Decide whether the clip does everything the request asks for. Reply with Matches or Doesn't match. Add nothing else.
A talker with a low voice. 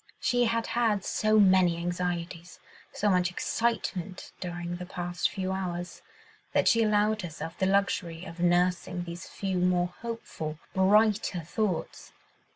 Doesn't match